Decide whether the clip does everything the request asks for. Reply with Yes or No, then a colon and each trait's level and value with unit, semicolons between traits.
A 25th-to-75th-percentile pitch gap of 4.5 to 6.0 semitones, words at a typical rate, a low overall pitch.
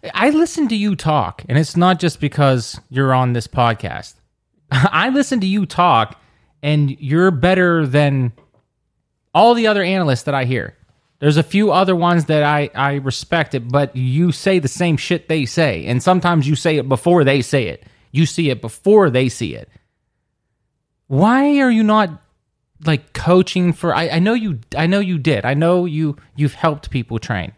No: average, 5.1 semitones; average, 185 wpm; medium, 150 Hz